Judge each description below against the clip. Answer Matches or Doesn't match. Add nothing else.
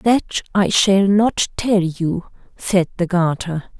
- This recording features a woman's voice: Matches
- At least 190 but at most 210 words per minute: Doesn't match